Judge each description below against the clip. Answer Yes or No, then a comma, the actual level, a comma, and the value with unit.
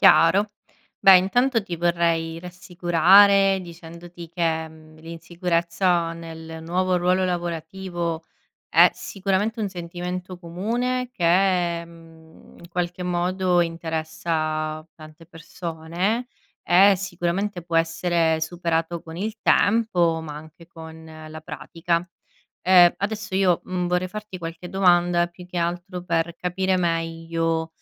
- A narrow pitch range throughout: Yes, narrow, 1.9 semitones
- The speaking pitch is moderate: Yes, medium, 175 Hz